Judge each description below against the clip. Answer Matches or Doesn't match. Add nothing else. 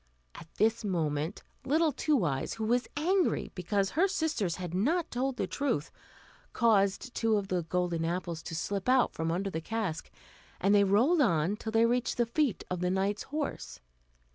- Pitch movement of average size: Doesn't match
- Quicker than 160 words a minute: Matches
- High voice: Matches